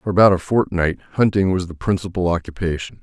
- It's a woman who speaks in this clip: No, male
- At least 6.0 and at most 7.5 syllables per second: Yes, 6.1 syllables/s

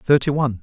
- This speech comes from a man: Yes, male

